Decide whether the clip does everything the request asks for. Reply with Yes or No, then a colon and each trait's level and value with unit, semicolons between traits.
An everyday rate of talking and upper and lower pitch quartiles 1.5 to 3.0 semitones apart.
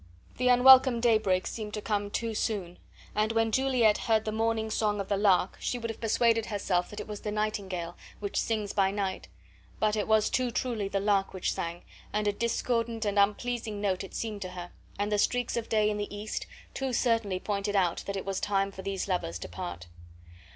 No: fast, 210 wpm; narrow, 2.5 semitones